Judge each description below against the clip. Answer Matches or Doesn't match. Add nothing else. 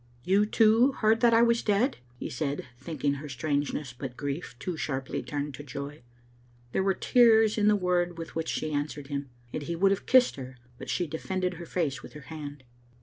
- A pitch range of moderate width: Doesn't match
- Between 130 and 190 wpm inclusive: Doesn't match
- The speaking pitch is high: Doesn't match